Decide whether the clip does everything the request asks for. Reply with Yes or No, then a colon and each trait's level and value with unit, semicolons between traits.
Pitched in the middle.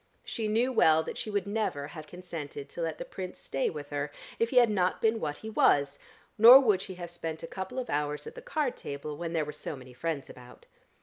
Yes: medium, 170 Hz